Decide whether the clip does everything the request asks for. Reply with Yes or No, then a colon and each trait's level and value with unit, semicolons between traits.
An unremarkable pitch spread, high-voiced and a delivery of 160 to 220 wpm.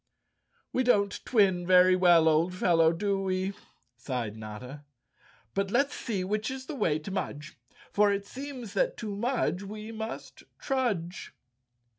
No: average, 4.7 semitones; high, 195 Hz; average, 145 wpm